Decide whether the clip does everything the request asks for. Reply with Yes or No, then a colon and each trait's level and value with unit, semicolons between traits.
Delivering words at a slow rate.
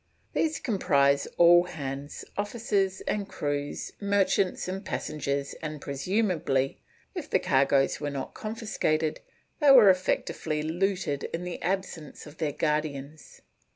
Yes: slow, 120 wpm